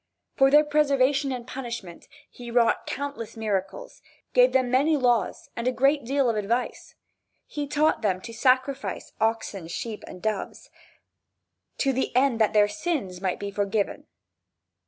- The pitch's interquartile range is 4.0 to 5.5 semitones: Yes, average, 4.5 semitones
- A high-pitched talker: Yes, high, 245 Hz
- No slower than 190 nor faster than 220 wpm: No, average, 150 wpm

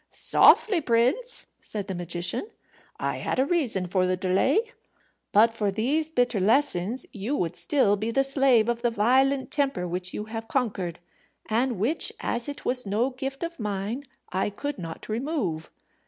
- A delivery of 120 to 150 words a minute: No, average, 165 wpm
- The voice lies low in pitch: No, high, 230 Hz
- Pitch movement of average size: No, wide, 5.7 semitones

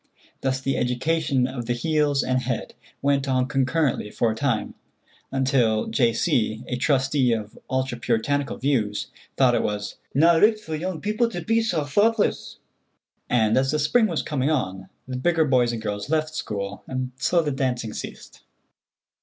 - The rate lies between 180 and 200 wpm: No, average, 170 wpm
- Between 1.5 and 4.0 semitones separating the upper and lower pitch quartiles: No, average, 4.4 semitones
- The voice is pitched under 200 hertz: Yes, low, 135 Hz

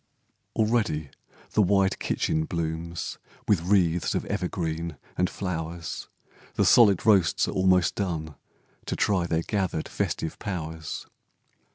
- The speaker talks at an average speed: No, slow, 120 wpm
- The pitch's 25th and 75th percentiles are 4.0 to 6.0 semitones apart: No, average, 3.3 semitones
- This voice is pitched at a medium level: No, very low, 85 Hz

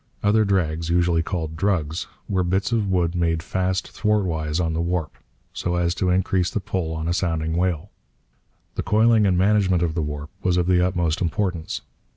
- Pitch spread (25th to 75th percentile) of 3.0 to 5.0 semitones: No, narrow, 2.5 semitones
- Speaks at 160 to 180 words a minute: No, average, 190 wpm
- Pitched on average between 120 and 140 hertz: No, very low, 90 Hz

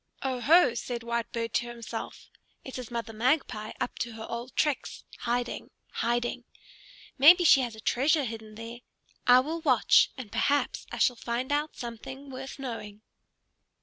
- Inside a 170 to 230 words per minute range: No, average, 150 wpm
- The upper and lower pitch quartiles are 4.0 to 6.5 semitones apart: No, narrow, 2.5 semitones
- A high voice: Yes, high, 240 Hz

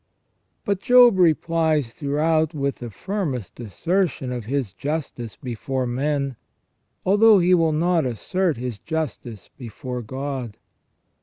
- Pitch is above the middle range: No, medium, 145 Hz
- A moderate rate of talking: No, slow, 120 wpm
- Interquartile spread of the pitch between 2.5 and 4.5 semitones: No, average, 5.1 semitones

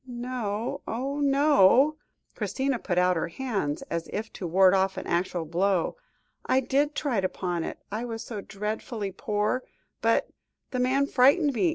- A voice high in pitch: Yes, high, 225 Hz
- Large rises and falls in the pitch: Yes, wide, 5.8 semitones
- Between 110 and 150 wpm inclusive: No, average, 165 wpm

